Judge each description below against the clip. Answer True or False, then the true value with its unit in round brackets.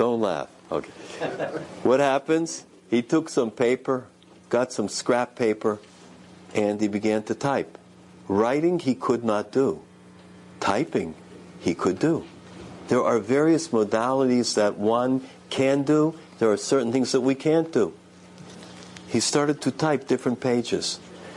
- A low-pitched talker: True (120 Hz)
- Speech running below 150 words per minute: True (140 wpm)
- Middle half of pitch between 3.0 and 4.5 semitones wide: False (5.2 semitones)